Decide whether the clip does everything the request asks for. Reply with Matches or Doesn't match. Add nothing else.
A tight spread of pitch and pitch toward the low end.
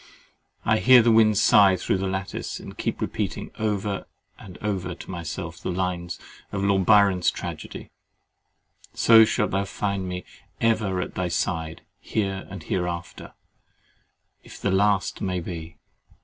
Matches